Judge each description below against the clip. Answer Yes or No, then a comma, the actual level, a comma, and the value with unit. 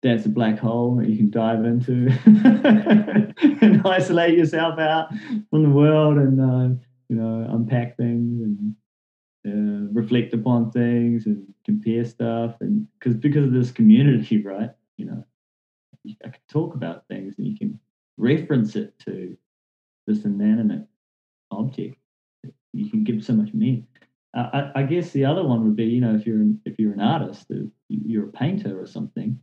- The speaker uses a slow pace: No, average, 170 wpm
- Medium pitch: No, low, 125 Hz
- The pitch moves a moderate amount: No, wide, 7.0 semitones